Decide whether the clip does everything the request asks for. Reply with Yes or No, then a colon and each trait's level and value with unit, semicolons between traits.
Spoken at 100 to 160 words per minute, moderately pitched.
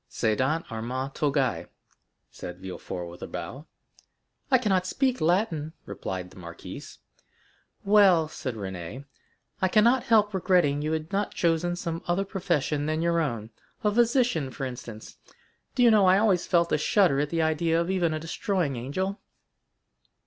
Yes: average, 150 wpm; medium, 160 Hz